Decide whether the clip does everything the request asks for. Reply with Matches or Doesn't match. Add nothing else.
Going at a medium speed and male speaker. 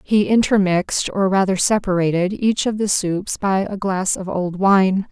Doesn't match